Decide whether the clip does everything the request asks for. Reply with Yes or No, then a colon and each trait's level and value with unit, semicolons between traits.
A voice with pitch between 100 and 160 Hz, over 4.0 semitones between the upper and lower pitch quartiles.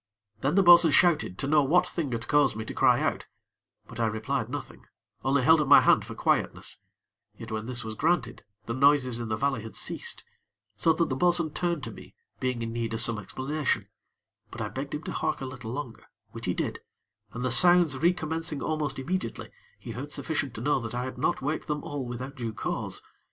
Yes: low, 135 Hz; average, 4.7 semitones